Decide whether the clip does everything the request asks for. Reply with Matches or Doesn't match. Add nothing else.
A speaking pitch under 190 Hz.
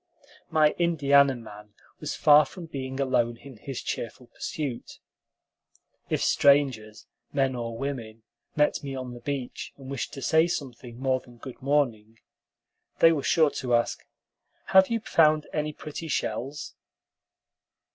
Matches